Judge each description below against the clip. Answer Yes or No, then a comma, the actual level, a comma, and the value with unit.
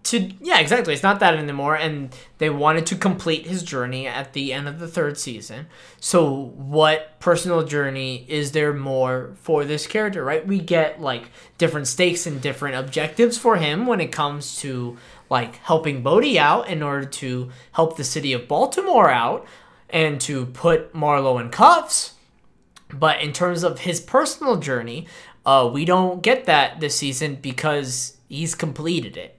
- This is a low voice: No, medium, 155 Hz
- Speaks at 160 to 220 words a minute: Yes, average, 170 wpm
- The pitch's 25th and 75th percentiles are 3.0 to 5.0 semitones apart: Yes, average, 4.0 semitones